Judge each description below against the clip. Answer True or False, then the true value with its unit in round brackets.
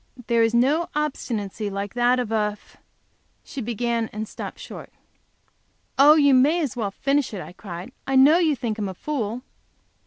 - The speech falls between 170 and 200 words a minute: True (180 wpm)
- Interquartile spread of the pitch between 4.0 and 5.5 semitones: True (4.9 semitones)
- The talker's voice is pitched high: True (240 Hz)